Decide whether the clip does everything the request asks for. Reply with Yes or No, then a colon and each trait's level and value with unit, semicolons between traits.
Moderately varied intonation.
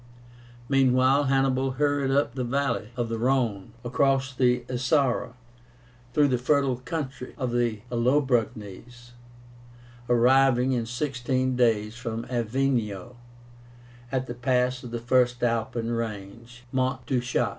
No: narrow, 2.1 semitones